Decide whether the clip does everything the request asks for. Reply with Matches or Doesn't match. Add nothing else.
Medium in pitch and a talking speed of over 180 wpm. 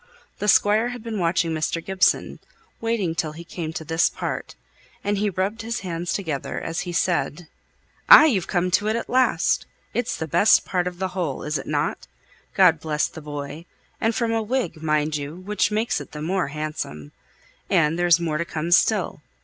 Matches